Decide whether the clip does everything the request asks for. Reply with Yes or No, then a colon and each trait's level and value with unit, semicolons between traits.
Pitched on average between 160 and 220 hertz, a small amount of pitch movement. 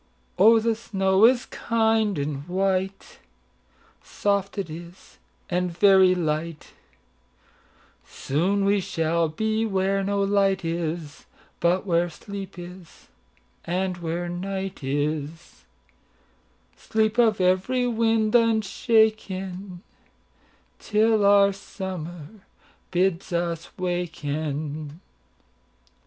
No: medium, 185 Hz; average, 3.3 semitones